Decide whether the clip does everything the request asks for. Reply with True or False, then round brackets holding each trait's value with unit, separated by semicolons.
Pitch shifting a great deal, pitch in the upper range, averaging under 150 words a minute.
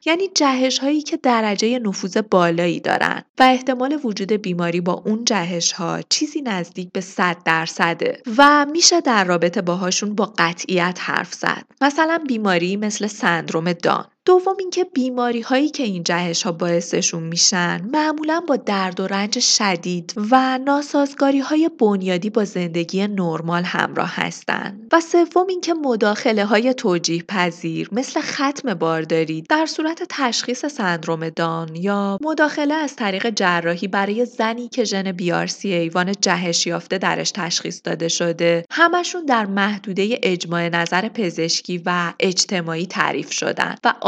True (7.0 semitones; 205 Hz; 140 wpm)